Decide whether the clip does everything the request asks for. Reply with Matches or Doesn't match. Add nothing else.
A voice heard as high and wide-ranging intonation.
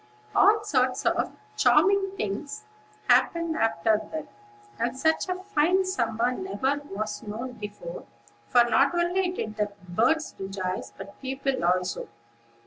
Matches